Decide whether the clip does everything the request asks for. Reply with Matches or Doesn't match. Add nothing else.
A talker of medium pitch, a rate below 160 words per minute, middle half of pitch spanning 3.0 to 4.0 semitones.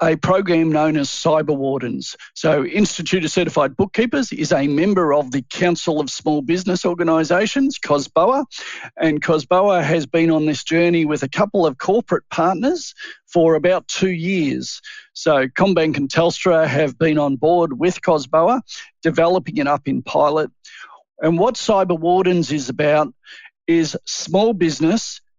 Matches